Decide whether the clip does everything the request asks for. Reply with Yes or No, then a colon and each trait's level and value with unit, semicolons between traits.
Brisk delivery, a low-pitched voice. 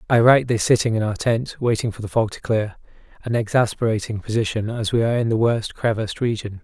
Yes: fast, 210 wpm; low, 115 Hz